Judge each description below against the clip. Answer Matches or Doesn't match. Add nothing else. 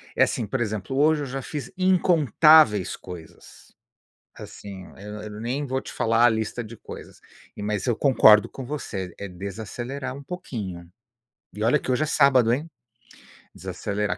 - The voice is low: Matches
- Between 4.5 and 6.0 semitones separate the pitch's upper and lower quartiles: Matches